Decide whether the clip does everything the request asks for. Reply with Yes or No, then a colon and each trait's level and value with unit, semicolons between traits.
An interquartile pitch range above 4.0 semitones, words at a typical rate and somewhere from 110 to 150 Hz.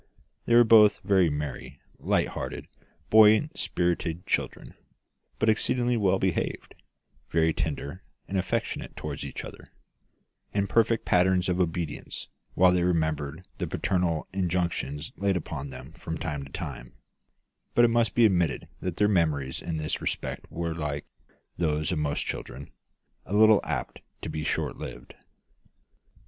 No: average, 4.5 semitones; average, 145 wpm; very low, 90 Hz